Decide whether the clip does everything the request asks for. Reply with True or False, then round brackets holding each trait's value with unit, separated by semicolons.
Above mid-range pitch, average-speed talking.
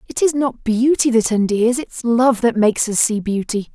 False (235 Hz; 210 wpm)